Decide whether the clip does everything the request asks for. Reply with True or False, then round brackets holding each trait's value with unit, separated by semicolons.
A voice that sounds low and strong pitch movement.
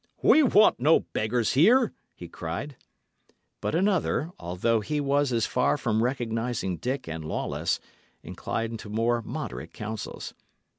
False (120 Hz; 4.9 semitones)